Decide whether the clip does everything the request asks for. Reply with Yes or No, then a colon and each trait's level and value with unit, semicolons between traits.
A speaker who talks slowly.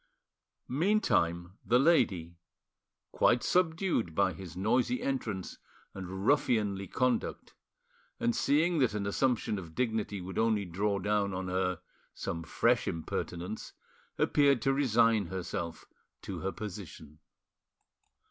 Yes: slow, 115 wpm